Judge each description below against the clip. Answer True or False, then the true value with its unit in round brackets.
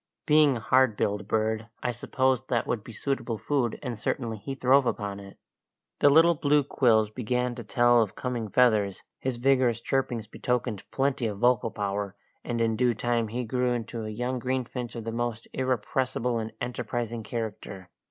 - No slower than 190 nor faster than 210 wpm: False (175 wpm)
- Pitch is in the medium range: False (120 Hz)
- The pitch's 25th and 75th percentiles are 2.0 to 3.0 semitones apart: True (2.6 semitones)